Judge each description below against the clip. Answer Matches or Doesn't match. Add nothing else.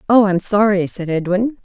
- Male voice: Doesn't match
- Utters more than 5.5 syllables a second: Doesn't match